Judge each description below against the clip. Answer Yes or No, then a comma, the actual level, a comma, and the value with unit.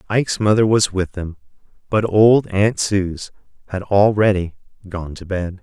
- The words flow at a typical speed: Yes, average, 150 wpm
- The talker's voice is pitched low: Yes, low, 100 Hz